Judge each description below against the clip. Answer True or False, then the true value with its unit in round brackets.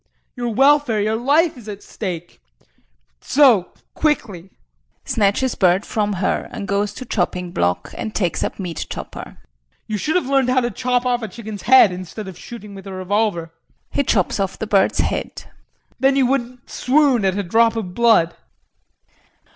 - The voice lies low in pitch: False (215 Hz)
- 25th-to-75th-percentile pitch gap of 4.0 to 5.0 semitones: True (4.7 semitones)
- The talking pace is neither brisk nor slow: True (170 wpm)